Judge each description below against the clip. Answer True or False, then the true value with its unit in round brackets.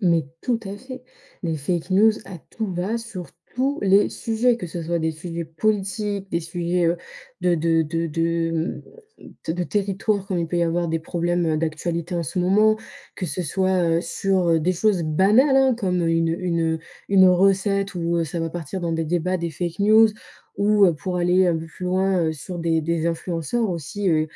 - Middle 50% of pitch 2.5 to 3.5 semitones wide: True (3.0 semitones)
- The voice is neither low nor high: True (175 Hz)